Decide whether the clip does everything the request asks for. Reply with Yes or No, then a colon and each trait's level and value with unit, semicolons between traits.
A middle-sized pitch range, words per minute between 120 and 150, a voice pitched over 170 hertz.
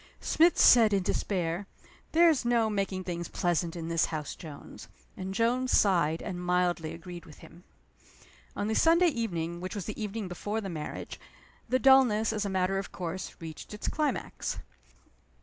No: average, 4.5 semitones; average, 165 wpm; high, 190 Hz